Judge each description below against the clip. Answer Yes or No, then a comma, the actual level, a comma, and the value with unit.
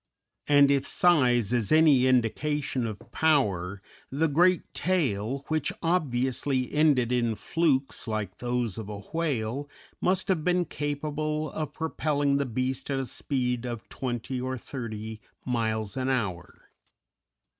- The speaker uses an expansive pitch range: No, average, 4.5 semitones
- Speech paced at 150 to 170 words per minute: No, slow, 135 wpm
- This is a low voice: Yes, low, 130 Hz